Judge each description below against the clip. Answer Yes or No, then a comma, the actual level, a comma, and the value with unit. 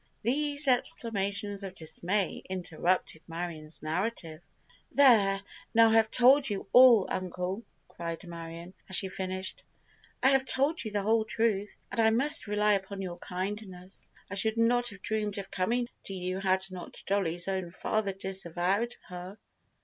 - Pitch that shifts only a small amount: No, average, 3.6 semitones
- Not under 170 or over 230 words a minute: No, average, 150 wpm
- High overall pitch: Yes, high, 195 Hz